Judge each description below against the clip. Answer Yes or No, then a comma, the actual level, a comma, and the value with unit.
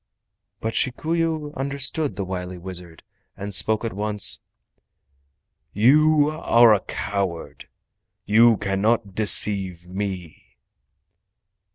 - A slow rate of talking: Yes, slow, 95 wpm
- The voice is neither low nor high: No, low, 105 Hz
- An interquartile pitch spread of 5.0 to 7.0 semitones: Yes, wide, 5.6 semitones